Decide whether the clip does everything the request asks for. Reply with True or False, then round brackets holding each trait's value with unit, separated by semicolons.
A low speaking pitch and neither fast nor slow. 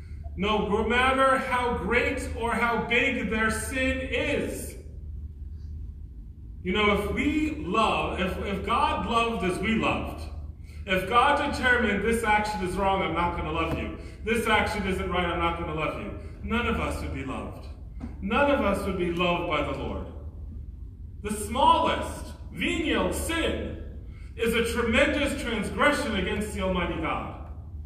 False (190 Hz; 155 wpm)